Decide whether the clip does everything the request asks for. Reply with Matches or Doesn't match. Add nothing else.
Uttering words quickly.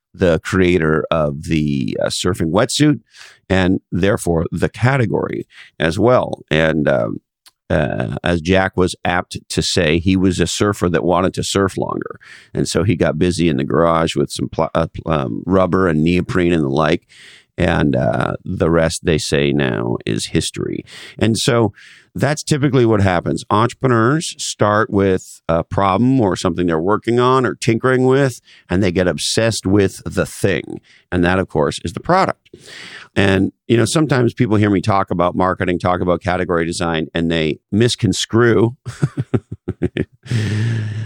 Doesn't match